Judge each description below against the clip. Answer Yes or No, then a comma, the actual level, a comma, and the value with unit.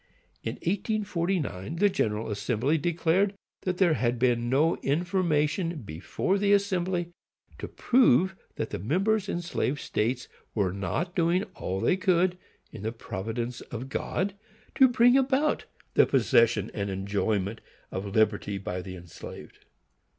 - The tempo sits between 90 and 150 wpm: Yes, average, 140 wpm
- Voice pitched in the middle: Yes, medium, 150 Hz